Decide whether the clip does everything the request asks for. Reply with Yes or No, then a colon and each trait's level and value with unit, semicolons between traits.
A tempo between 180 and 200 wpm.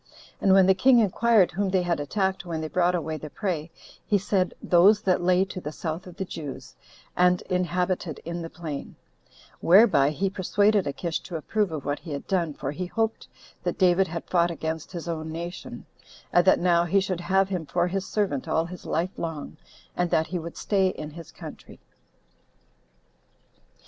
Yes: average, 190 wpm